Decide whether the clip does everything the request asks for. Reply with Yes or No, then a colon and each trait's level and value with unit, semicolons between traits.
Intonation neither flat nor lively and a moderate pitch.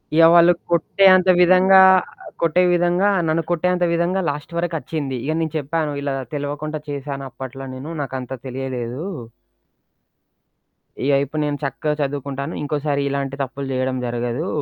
Yes: average, 3.8 semitones; medium, 145 Hz